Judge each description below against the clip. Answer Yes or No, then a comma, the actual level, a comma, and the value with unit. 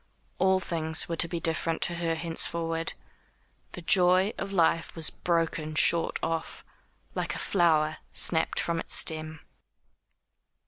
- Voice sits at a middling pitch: Yes, medium, 165 Hz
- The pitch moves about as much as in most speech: No, narrow, 1.2 semitones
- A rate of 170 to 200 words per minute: No, slow, 135 wpm